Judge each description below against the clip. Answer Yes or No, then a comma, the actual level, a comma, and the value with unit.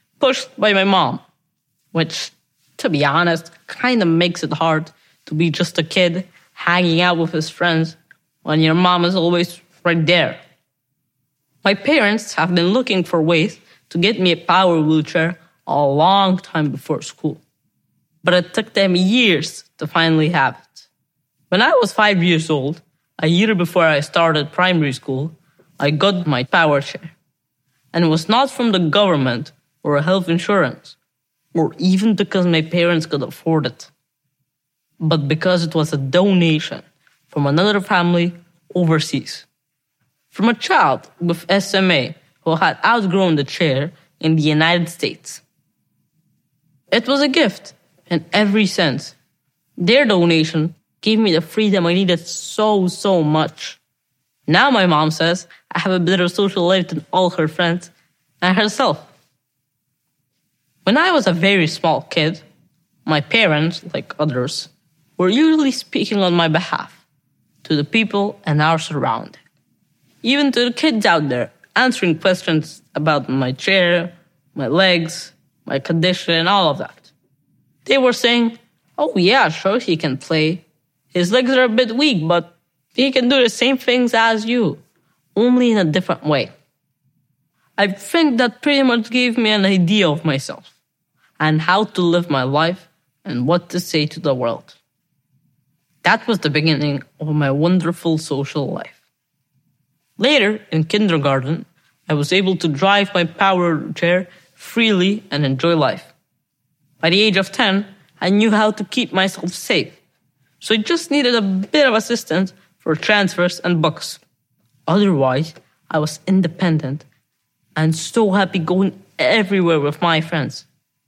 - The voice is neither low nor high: Yes, medium, 170 Hz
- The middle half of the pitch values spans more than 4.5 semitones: No, average, 3.9 semitones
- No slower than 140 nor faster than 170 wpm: Yes, average, 150 wpm